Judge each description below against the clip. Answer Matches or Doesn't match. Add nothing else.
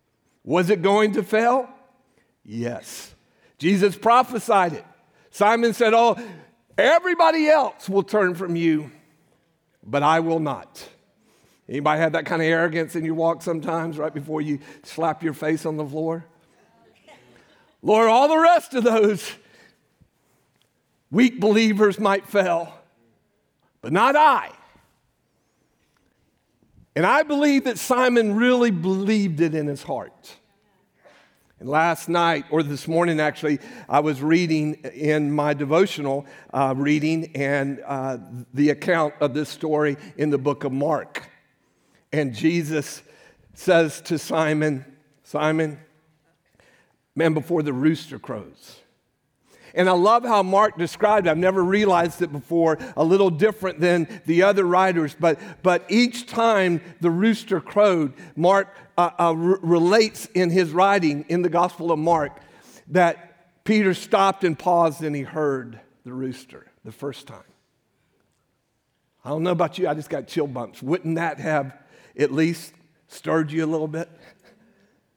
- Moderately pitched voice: Matches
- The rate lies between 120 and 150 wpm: Matches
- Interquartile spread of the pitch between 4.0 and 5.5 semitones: Matches